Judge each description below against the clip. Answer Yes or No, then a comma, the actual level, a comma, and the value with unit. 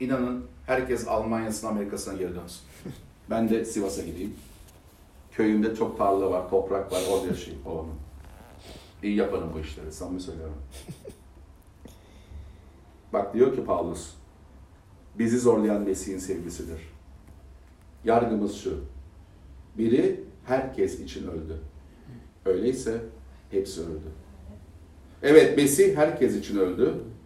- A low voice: Yes, very low, 90 Hz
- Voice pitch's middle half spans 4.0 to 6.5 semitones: Yes, wide, 5.4 semitones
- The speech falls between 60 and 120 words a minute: Yes, average, 105 wpm